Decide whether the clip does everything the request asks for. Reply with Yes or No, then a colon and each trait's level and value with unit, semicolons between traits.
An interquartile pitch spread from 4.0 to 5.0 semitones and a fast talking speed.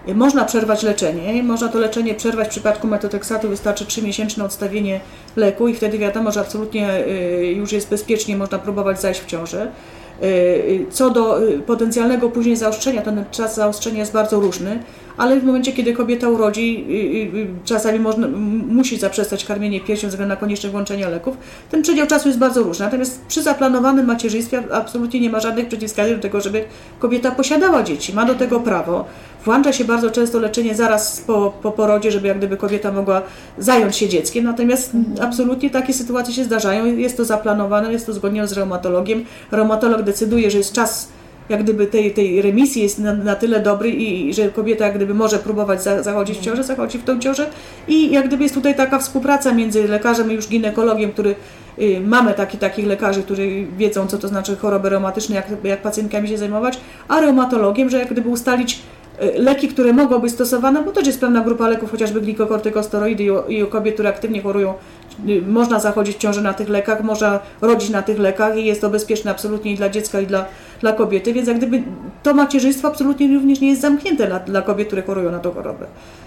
No: average, 2.8 semitones; fast, 190 wpm